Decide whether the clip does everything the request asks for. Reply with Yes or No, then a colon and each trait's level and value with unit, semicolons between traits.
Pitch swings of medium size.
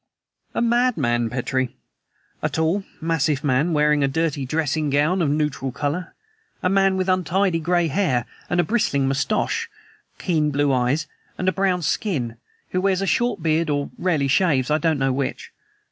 Yes: average, 4.7 semitones